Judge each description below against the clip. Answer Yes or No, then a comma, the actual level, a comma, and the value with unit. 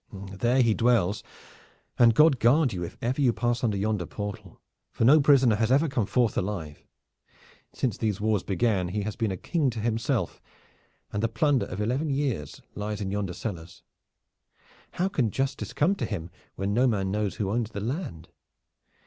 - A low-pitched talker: Yes, low, 110 Hz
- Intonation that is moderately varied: Yes, average, 4.3 semitones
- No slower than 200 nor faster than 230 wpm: No, average, 185 wpm